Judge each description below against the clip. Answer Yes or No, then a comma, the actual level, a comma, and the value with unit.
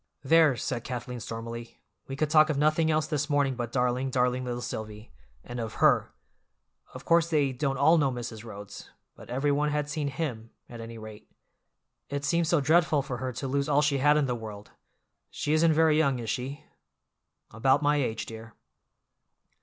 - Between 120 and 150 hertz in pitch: Yes, low, 135 Hz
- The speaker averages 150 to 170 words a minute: No, average, 185 wpm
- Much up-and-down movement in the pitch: No, average, 3.8 semitones